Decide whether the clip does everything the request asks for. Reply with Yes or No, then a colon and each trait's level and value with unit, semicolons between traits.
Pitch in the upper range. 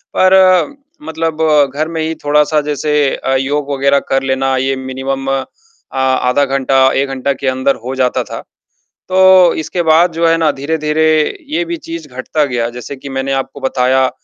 No: medium, 140 Hz